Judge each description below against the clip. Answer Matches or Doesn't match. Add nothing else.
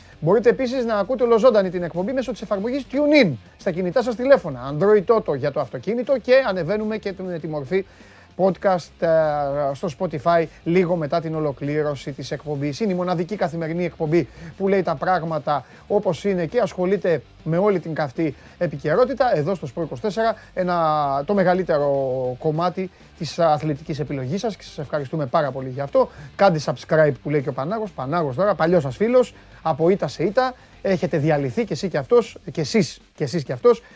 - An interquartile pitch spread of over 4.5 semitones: Matches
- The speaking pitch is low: Doesn't match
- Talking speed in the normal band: Doesn't match